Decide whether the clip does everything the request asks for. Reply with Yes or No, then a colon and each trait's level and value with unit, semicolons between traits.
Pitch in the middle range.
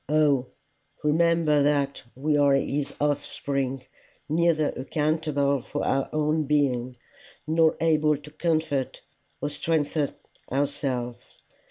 Yes: medium, 145 Hz